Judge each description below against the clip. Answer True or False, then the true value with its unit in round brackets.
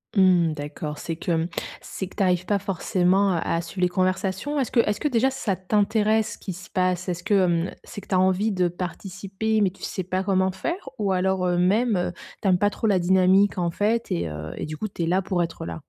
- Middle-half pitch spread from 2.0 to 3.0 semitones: True (2.4 semitones)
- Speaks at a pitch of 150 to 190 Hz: True (185 Hz)